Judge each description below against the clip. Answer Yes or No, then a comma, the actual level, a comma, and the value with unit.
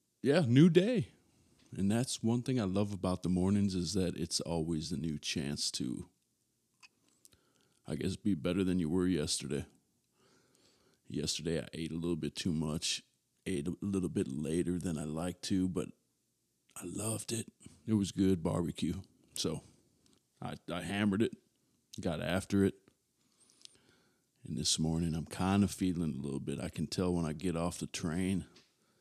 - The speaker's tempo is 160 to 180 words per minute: Yes, average, 165 wpm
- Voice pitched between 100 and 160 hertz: No, very low, 90 Hz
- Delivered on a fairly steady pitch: No, average, 3.4 semitones